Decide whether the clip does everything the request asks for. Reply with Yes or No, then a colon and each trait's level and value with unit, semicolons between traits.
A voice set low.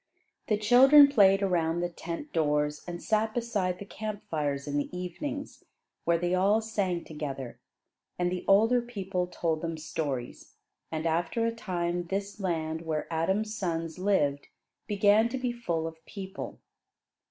No: medium, 180 Hz